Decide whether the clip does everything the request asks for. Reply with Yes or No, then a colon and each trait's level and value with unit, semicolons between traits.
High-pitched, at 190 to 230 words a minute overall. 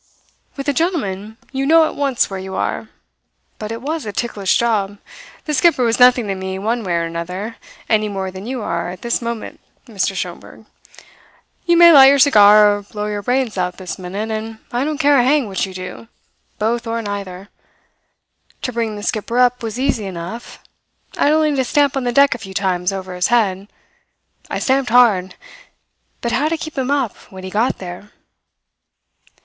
Yes: high, 220 Hz; average, 195 wpm